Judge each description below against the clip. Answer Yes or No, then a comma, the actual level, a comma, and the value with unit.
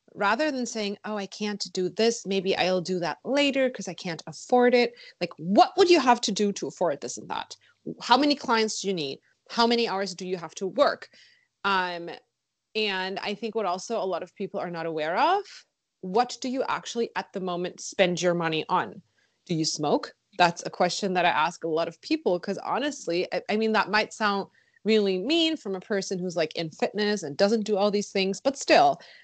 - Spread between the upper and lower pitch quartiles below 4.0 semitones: No, average, 4.4 semitones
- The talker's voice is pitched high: Yes, high, 200 Hz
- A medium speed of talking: No, fast, 220 wpm